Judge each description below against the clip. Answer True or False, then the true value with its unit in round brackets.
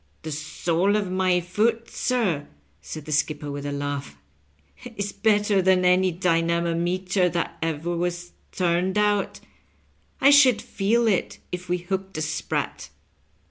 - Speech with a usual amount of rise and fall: True (3.6 semitones)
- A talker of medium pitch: True (180 Hz)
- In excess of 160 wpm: False (145 wpm)